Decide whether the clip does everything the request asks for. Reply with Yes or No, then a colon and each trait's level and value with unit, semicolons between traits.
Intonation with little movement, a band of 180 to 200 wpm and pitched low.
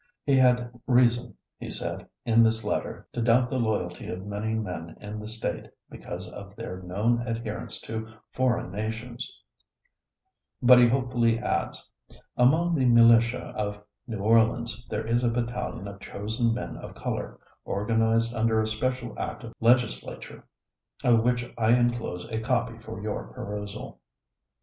No: narrow, 2.1 semitones; average, 150 wpm; low, 115 Hz